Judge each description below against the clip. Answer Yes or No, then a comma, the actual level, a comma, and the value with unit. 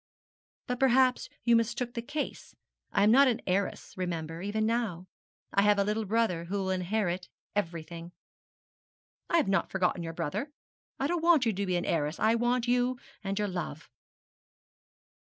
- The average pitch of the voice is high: Yes, high, 205 Hz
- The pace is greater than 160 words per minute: Yes, average, 170 wpm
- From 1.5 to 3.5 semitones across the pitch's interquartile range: No, average, 5.1 semitones